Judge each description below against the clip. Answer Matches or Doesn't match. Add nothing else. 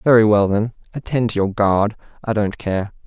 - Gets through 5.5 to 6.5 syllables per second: Doesn't match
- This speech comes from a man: Matches